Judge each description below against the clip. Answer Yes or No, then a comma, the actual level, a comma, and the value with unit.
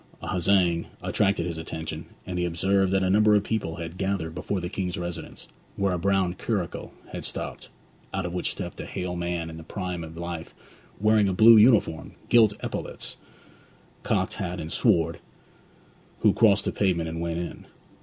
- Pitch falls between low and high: No, very low, 90 Hz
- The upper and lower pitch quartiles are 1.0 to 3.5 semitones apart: Yes, average, 2.8 semitones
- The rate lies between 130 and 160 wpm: No, average, 180 wpm